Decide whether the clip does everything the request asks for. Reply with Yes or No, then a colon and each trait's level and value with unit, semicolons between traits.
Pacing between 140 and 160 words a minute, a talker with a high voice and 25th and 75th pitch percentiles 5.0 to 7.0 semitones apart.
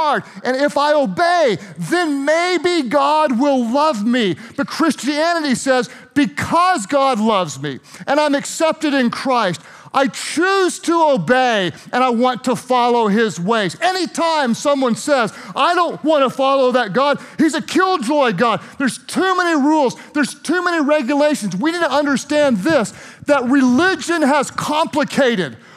No: average, 150 wpm; very high, 280 Hz; average, 4.2 semitones